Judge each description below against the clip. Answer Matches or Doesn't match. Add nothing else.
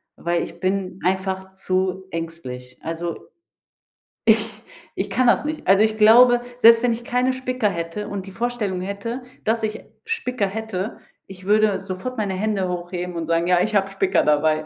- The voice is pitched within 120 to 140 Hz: Doesn't match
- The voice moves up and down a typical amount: Matches